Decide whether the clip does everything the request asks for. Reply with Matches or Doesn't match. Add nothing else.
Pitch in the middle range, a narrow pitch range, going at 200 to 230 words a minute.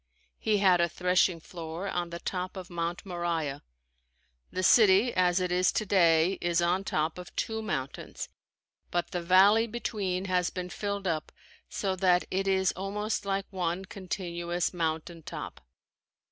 Doesn't match